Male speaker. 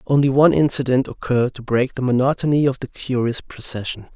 Yes: male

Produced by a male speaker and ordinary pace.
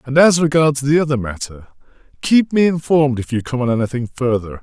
Yes: male; average, 180 wpm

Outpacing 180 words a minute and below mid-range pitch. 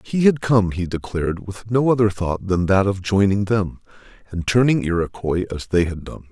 Yes: average, 200 wpm; low, 100 Hz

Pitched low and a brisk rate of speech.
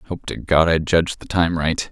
Yes: very low, 80 Hz; fast, 250 wpm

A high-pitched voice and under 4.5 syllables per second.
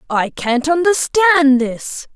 Yes: very high, 290 Hz; 3.2 syllables/s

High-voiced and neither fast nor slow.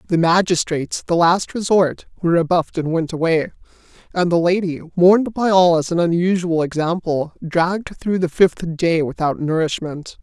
No: medium, 170 Hz; average, 160 wpm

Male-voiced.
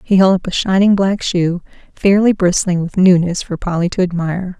No: female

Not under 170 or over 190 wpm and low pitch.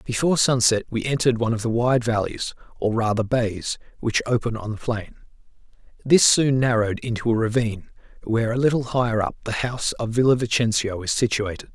Yes: average, 180 wpm; low, 115 Hz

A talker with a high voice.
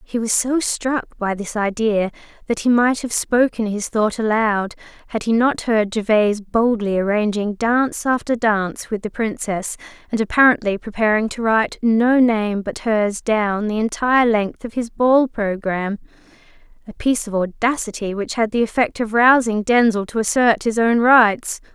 Yes: high, 220 Hz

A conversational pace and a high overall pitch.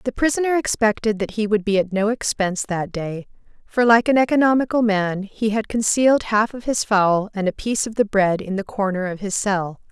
No: fast, 220 wpm; high, 210 Hz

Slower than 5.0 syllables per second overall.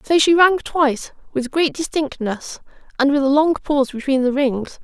Yes: 4.8 syllables/s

